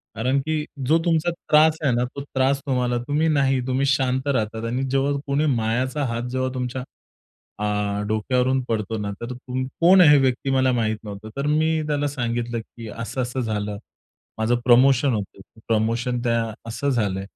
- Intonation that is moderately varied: Yes, average, 3.4 semitones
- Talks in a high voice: No, low, 125 Hz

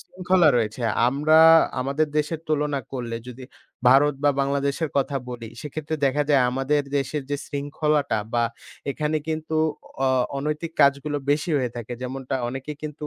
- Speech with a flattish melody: Yes, narrow, 2.2 semitones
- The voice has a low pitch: No, medium, 145 Hz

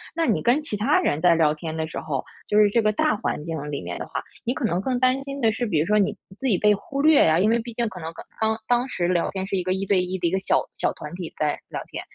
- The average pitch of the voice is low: No, high, 195 Hz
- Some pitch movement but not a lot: No, wide, 6.1 semitones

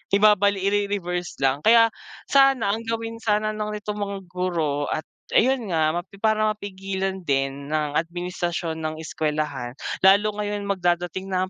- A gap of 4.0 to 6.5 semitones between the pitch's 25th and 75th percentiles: Yes, average, 4.4 semitones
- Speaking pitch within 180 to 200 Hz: Yes, high, 190 Hz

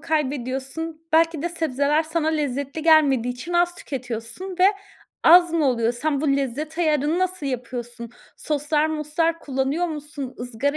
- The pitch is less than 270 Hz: No, very high, 300 Hz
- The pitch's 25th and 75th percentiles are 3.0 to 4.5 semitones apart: Yes, average, 3.7 semitones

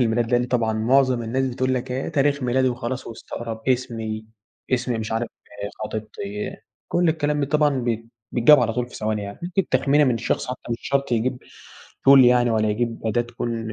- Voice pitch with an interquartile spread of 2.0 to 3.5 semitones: Yes, average, 2.7 semitones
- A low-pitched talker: Yes, low, 120 Hz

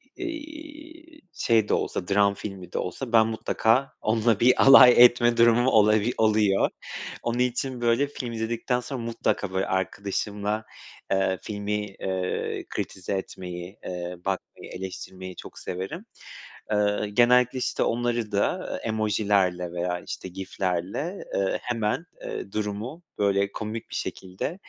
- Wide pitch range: No, average, 4.0 semitones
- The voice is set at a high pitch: No, low, 110 Hz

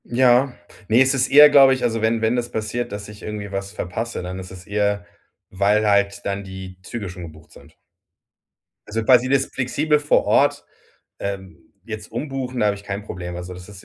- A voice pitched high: No, low, 105 Hz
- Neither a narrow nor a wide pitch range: Yes, average, 4.0 semitones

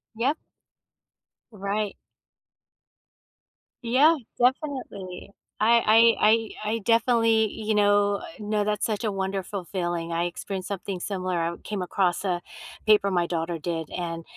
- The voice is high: Yes, high, 200 Hz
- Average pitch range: Yes, average, 3.6 semitones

